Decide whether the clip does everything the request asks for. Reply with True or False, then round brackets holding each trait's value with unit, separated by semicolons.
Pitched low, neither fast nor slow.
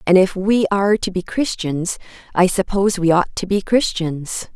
False (190 Hz; 185 wpm)